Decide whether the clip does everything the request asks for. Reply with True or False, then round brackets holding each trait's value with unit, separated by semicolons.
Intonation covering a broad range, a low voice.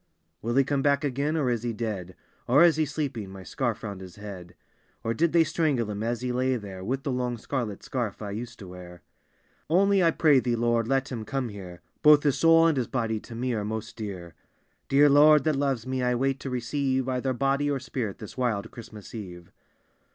False (4.4 semitones; 125 Hz)